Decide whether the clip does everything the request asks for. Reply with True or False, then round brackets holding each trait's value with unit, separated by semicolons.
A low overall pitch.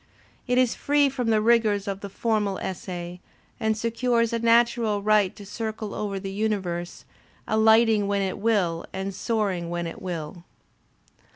False (210 Hz)